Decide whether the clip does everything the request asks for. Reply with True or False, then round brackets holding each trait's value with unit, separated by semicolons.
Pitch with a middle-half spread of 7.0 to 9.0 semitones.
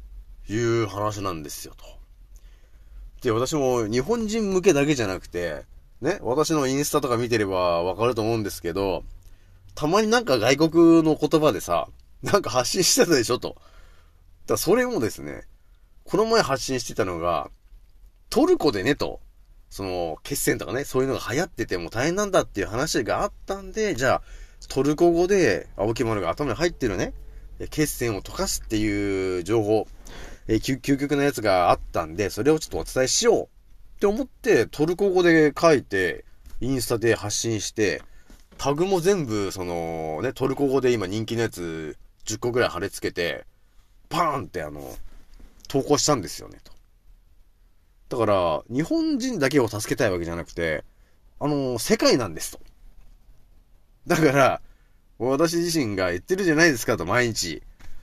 True (8.6 semitones)